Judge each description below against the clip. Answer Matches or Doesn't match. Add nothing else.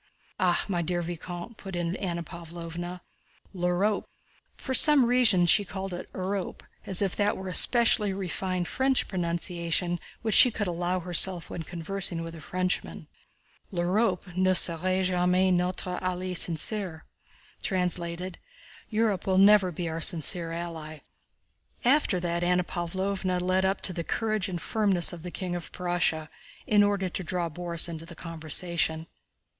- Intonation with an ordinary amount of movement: Doesn't match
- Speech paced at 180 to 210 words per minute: Doesn't match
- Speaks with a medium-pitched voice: Matches